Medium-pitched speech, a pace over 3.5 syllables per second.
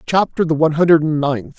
Yes: medium, 160 Hz; 6.1 syllables/s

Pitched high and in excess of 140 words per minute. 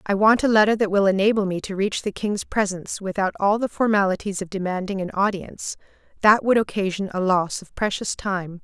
Yes: high, 200 Hz; average, 200 wpm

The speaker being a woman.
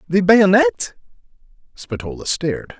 No: male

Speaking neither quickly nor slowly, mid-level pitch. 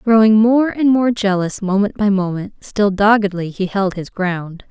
No: average, 180 wpm; high, 205 Hz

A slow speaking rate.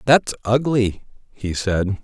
Yes: slow, 120 wpm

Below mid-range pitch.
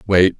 Yes: very low, 95 Hz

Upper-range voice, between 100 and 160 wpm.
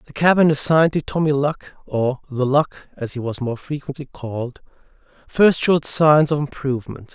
No: medium, 140 Hz; average, 150 wpm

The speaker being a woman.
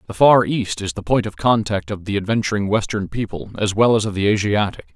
No: male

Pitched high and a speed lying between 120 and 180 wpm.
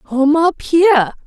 Yes: very high, 300 Hz; average, 140 wpm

